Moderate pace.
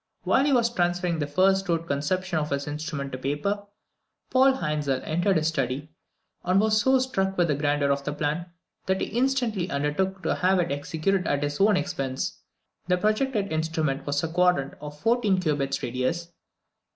Yes: average, 175 wpm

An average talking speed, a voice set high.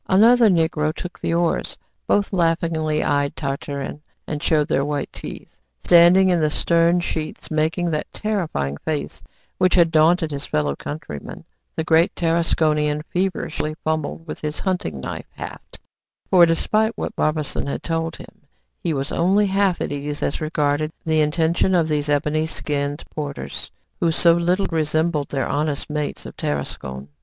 No: average, 155 wpm; medium, 155 Hz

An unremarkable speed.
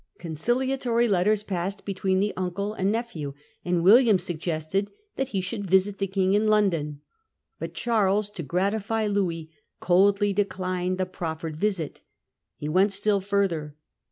Yes: average, 145 wpm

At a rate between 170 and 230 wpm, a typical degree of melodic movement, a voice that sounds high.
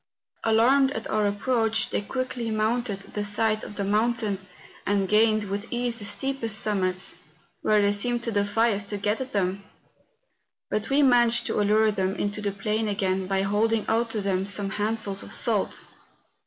No: average, 180 wpm; narrow, 2.2 semitones; high, 215 Hz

